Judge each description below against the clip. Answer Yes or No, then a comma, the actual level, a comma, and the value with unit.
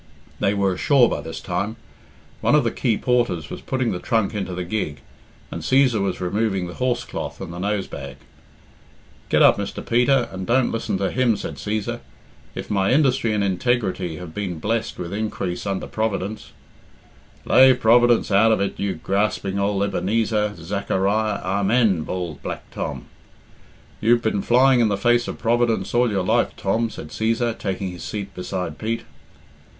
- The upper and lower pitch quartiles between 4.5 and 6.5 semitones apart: No, average, 3.6 semitones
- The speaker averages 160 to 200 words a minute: Yes, average, 175 wpm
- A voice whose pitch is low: Yes, low, 105 Hz